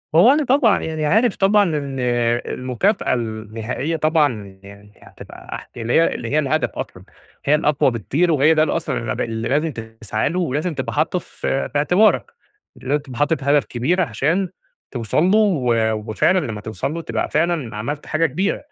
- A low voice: No, medium, 145 Hz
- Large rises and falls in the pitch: Yes, wide, 5.9 semitones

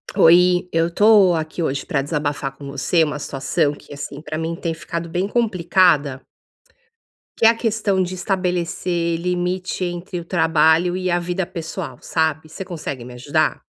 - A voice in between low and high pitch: Yes, medium, 170 Hz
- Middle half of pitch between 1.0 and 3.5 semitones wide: Yes, average, 2.7 semitones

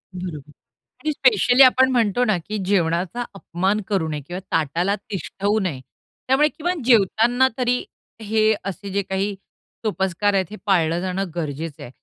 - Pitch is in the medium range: No, high, 195 Hz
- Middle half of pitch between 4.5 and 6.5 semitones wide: Yes, average, 5.0 semitones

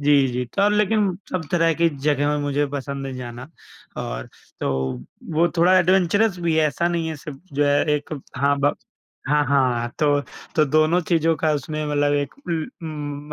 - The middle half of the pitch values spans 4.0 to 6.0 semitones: No, average, 3.0 semitones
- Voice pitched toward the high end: No, medium, 150 Hz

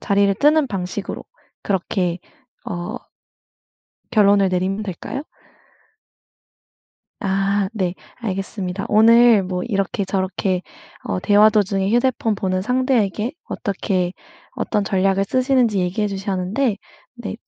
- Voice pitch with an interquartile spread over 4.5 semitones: No, average, 2.9 semitones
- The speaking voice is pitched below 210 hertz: Yes, high, 200 Hz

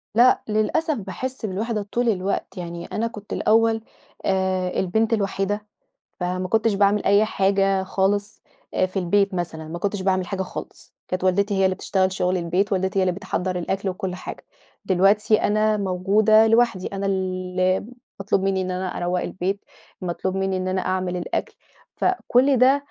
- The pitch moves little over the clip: Yes, narrow, 2.3 semitones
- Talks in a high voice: Yes, high, 195 Hz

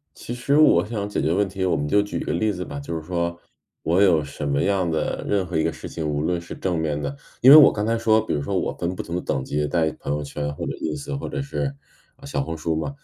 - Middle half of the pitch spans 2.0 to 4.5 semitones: No, average, 5.0 semitones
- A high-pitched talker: No, very low, 85 Hz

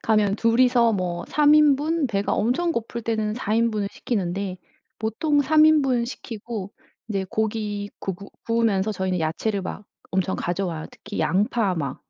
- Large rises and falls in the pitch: No, average, 3.7 semitones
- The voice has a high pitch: Yes, high, 215 Hz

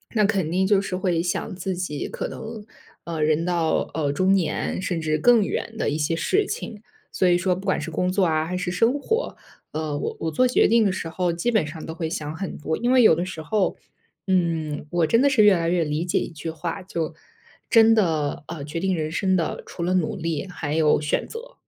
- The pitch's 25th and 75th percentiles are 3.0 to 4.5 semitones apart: Yes, average, 3.6 semitones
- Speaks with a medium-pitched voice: Yes, medium, 175 Hz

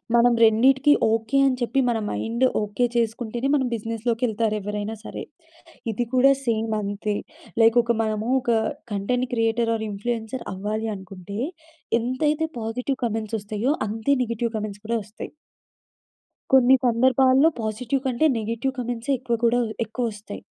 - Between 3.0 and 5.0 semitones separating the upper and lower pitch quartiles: No, narrow, 2.5 semitones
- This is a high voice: Yes, high, 230 Hz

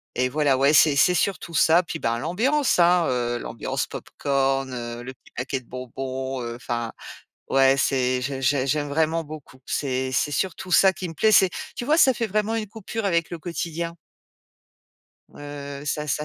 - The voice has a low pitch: No, medium, 145 Hz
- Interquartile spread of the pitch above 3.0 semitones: Yes, average, 4.8 semitones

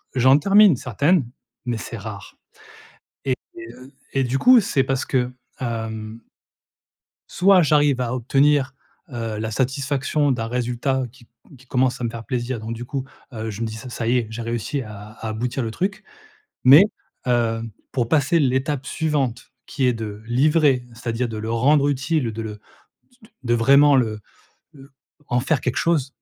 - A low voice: Yes, low, 125 Hz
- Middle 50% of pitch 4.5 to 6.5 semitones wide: No, average, 3.3 semitones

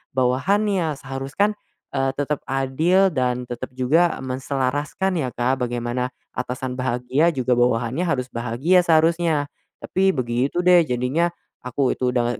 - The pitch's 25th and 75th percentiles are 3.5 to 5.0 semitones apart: Yes, average, 4.7 semitones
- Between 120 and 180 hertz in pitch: Yes, low, 135 Hz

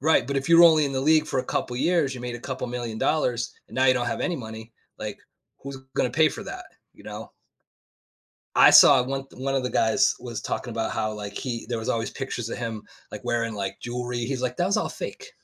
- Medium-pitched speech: No, low, 125 Hz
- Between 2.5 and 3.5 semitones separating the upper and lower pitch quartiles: Yes, average, 2.8 semitones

